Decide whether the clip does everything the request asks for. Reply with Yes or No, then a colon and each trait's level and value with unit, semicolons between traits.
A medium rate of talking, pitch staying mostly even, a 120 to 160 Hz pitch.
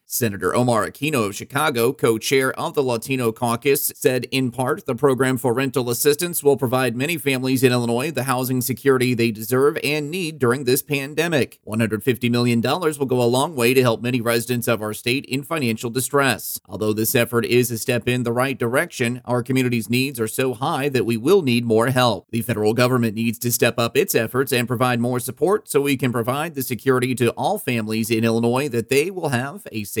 No: fast, 210 wpm; narrow, 2.3 semitones; low, 125 Hz